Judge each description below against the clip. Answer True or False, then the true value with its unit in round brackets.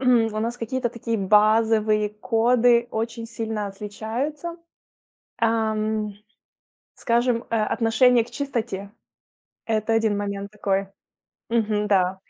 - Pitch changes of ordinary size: False (1.9 semitones)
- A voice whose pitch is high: True (225 Hz)